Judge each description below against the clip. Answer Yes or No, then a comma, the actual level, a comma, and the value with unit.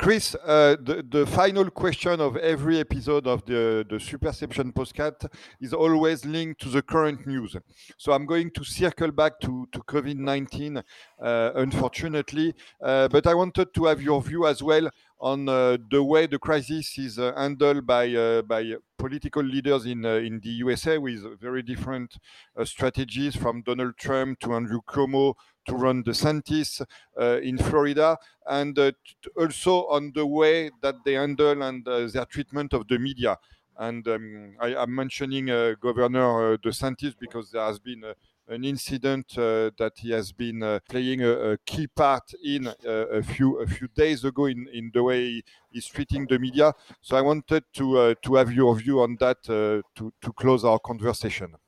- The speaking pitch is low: Yes, low, 130 Hz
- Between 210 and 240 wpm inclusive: No, average, 180 wpm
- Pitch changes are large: No, average, 3.7 semitones